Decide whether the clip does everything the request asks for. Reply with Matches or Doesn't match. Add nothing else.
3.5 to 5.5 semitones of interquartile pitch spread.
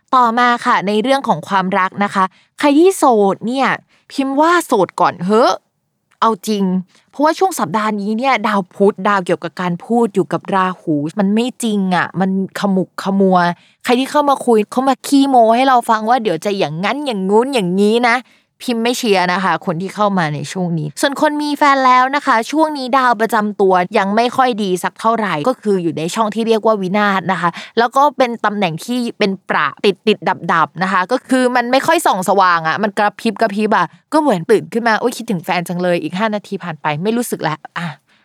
Matches